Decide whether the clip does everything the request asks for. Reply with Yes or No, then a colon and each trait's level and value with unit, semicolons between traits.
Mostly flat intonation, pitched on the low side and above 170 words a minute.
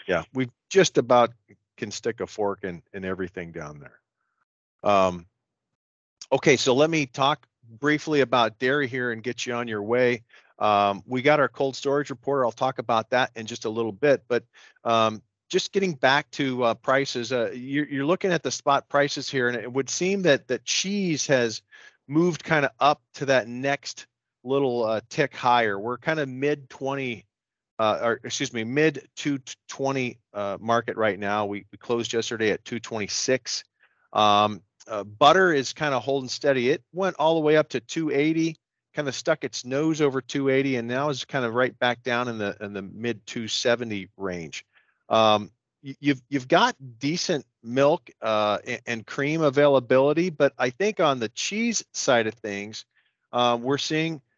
No: average, 4.2 semitones; low, 130 Hz; average, 180 wpm